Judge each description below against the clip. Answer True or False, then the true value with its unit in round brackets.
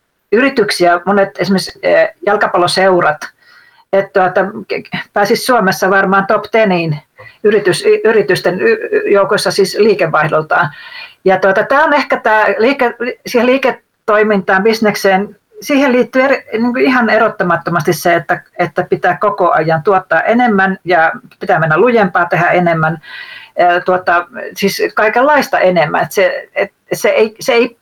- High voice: True (205 Hz)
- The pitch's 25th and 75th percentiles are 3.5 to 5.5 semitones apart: True (5.1 semitones)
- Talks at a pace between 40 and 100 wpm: False (125 wpm)